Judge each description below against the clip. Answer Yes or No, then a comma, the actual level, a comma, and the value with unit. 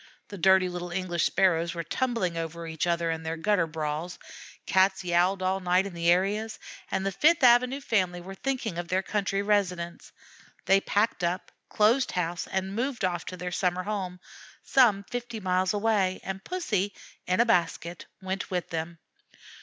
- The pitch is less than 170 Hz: No, medium, 185 Hz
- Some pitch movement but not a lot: Yes, average, 3.0 semitones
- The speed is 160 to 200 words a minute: Yes, average, 170 wpm